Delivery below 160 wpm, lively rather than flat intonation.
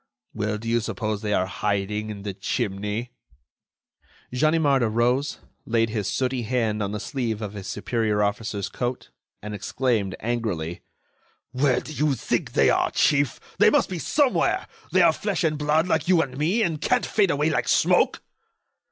No: average, 170 wpm; wide, 5.7 semitones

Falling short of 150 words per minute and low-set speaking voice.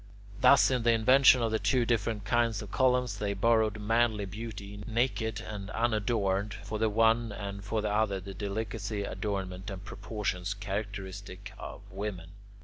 No: average, 155 wpm; low, 105 Hz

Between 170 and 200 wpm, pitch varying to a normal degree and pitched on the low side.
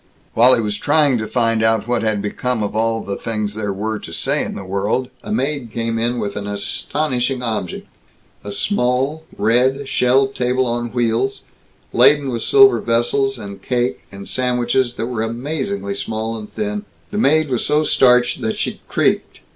Yes: average, 180 wpm; average, 3.3 semitones; low, 120 Hz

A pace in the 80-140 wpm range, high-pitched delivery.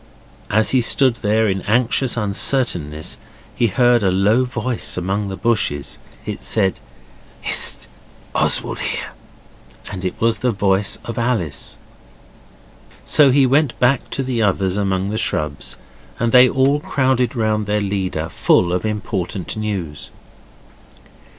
No: slow, 135 wpm; low, 110 Hz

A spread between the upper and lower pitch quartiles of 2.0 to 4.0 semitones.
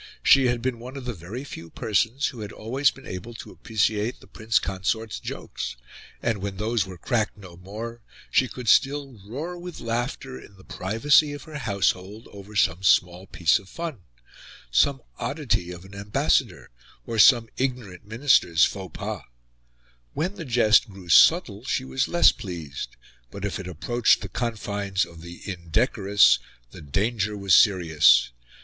No: average, 4.8 semitones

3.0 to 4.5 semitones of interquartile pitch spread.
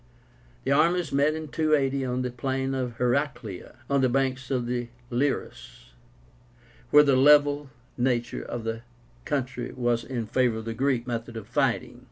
No: narrow, 2.6 semitones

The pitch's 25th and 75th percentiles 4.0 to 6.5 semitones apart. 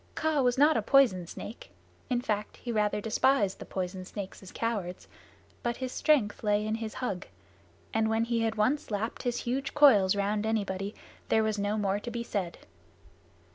No: average, 3.0 semitones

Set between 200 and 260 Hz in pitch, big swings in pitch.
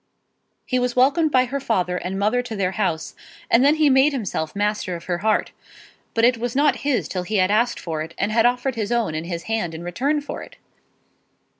Yes: high, 225 Hz; wide, 5.7 semitones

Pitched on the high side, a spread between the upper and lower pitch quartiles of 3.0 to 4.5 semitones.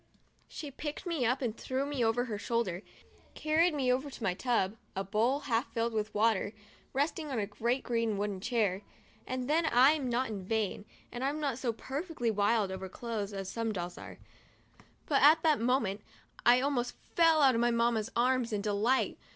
Yes: high, 235 Hz; average, 4.2 semitones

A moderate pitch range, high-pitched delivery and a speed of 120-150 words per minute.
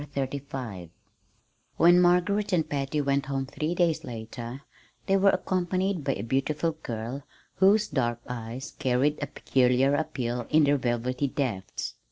No: average, 5.0 semitones; medium, 140 Hz; average, 145 wpm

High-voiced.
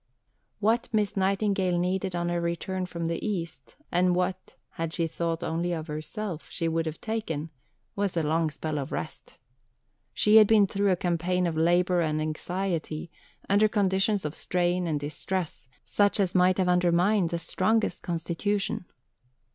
No: medium, 180 Hz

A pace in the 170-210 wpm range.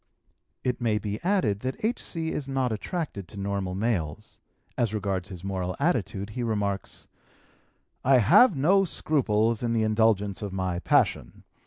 No: average, 150 wpm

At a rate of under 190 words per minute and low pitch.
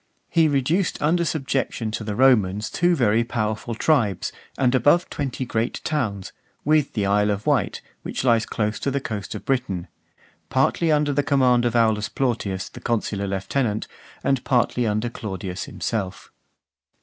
Yes: average, 155 wpm; low, 120 Hz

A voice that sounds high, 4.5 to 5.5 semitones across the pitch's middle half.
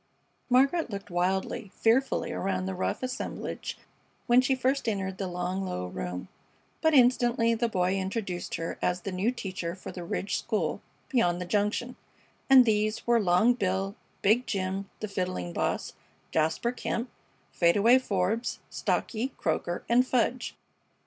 Yes: high, 200 Hz; average, 5.1 semitones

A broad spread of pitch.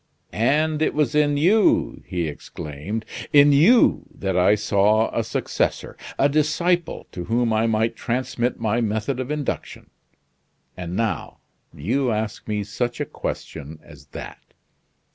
Yes: wide, 5.7 semitones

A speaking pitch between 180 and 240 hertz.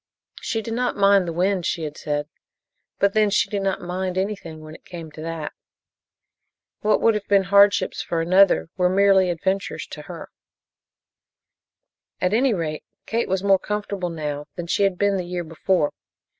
Yes: high, 190 Hz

